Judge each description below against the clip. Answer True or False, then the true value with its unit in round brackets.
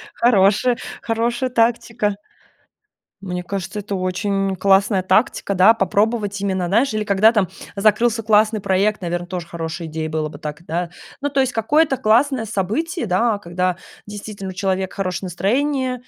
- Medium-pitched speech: False (200 Hz)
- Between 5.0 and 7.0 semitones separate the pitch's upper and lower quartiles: False (3.7 semitones)